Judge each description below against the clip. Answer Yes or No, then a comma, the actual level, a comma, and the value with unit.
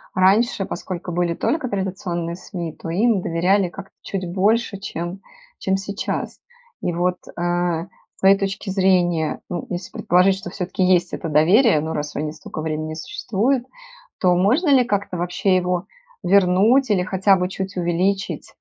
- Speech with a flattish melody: Yes, narrow, 2.3 semitones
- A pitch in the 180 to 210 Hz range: Yes, medium, 185 Hz